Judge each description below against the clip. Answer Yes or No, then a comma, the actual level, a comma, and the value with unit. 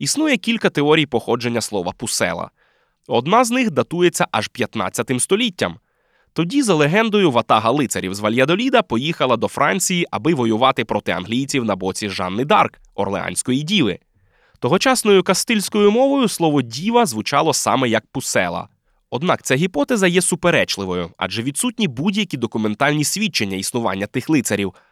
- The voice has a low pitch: No, medium, 145 Hz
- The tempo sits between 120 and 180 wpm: Yes, average, 130 wpm